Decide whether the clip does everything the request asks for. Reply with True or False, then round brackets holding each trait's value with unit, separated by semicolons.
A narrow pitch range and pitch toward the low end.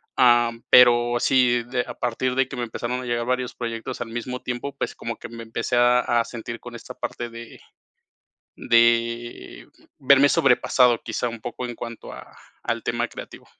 True (1.2 semitones; 120 Hz)